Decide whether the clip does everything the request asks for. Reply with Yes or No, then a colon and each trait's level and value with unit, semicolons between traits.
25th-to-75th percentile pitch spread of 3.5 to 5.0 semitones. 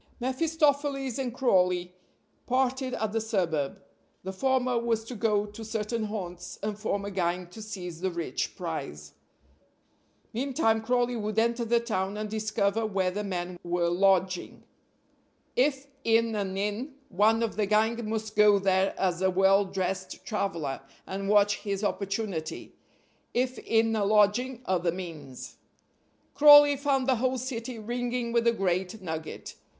Yes: average, 4.0 semitones